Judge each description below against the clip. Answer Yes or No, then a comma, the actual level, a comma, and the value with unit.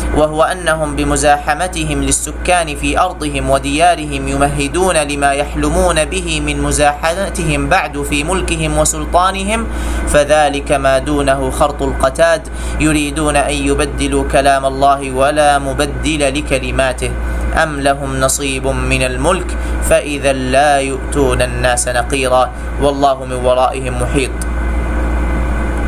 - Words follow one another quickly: No, average, 100 wpm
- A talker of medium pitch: Yes, medium, 145 Hz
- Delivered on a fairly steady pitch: Yes, narrow, 2.3 semitones